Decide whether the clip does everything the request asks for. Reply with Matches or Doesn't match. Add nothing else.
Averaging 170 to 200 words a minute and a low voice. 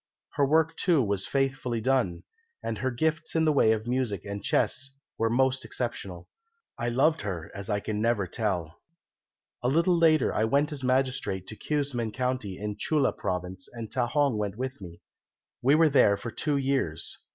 Matches